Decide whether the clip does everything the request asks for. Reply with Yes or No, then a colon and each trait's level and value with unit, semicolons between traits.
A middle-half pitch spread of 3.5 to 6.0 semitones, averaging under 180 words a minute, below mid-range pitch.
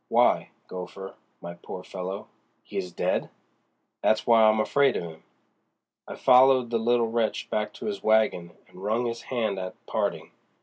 Yes: average, 4.1 semitones; average, 165 wpm; low, 110 Hz